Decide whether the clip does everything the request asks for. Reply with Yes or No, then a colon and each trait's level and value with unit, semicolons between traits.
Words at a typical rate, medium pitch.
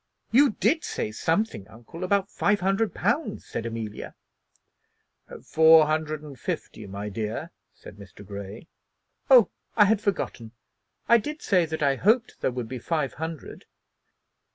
Yes: average, 145 wpm; medium, 160 Hz